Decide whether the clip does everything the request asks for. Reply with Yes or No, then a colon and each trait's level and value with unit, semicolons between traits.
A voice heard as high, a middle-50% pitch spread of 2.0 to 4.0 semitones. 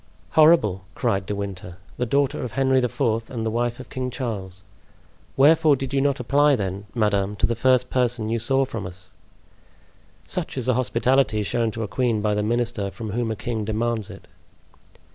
No: low, 115 Hz; average, 3.7 semitones